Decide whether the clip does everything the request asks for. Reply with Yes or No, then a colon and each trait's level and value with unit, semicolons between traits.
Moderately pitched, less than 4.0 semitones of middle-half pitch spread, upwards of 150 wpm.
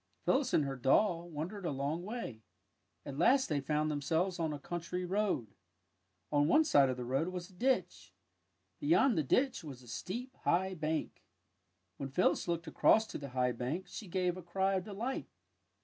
No: medium, 170 Hz; average, 5.3 semitones; average, 180 wpm